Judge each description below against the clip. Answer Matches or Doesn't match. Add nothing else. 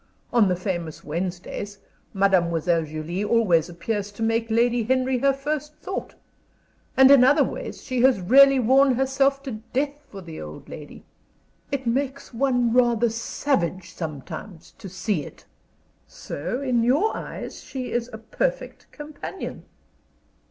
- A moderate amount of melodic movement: Doesn't match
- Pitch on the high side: Matches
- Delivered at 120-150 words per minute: Matches